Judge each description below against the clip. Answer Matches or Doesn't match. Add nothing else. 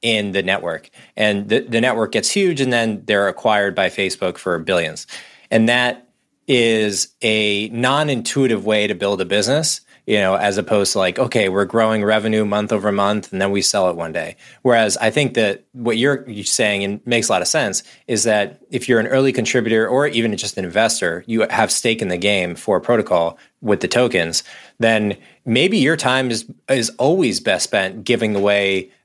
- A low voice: Matches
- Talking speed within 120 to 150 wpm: Doesn't match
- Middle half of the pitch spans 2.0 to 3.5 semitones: Matches